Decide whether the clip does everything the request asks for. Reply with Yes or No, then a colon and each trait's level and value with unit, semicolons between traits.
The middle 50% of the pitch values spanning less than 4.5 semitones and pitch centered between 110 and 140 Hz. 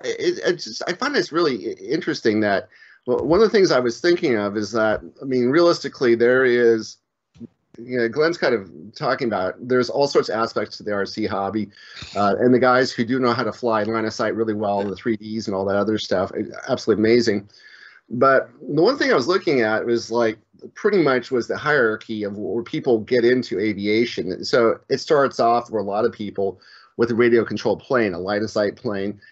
Yes: average, 2.7 semitones; low, 115 Hz